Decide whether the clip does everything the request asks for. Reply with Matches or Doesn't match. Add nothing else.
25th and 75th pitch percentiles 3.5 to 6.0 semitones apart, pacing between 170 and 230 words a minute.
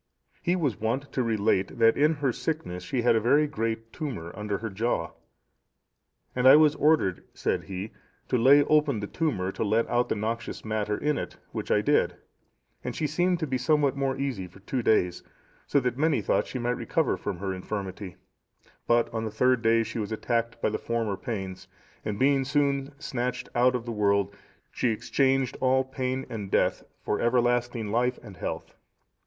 Matches